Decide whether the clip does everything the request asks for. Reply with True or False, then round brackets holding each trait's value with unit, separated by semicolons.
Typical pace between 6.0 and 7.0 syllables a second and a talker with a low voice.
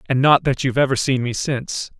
True (6.3 syllables/s; 130 Hz)